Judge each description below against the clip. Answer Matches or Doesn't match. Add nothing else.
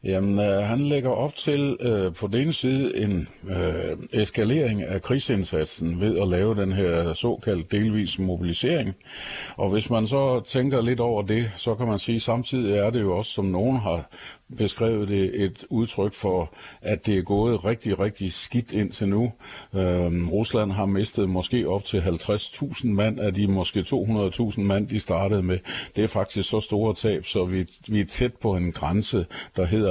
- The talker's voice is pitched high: Doesn't match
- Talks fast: Doesn't match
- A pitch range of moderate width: Matches